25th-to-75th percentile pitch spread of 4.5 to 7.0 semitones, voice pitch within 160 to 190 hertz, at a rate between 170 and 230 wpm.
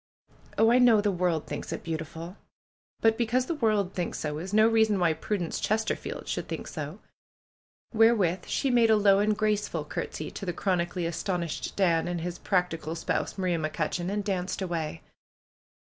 No: average, 4.1 semitones; medium, 185 Hz; average, 180 wpm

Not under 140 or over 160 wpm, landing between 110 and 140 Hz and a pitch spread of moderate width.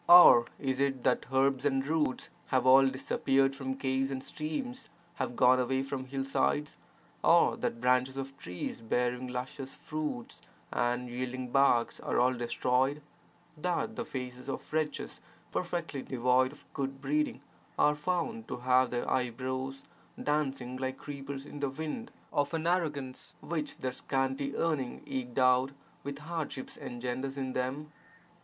No: average, 145 wpm; low, 135 Hz; narrow, 2.2 semitones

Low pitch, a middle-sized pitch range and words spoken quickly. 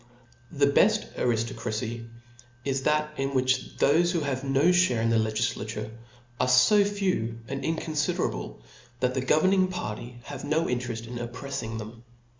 No: low, 130 Hz; average, 4.9 semitones; average, 155 wpm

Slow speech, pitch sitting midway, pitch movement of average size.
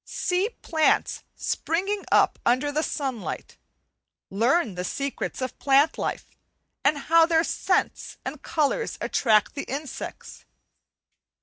No: slow, 115 wpm; very high, 290 Hz; average, 4.1 semitones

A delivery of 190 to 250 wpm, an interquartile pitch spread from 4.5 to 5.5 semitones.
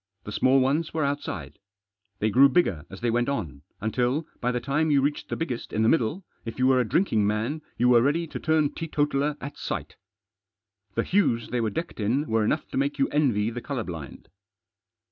Yes: fast, 205 wpm; average, 4.9 semitones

